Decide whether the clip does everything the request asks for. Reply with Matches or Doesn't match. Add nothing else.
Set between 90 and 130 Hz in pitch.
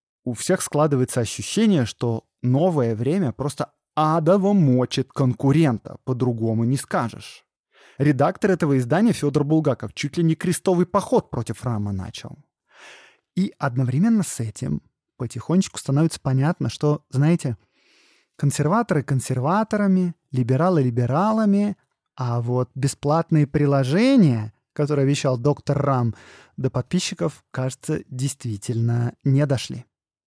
Doesn't match